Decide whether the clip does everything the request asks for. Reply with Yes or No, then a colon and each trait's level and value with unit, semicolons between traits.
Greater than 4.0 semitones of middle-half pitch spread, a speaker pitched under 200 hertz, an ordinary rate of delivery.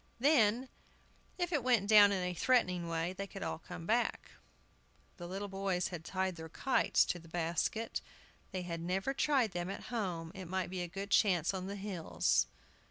No: average, 3.3 semitones; high, 190 Hz; average, 185 wpm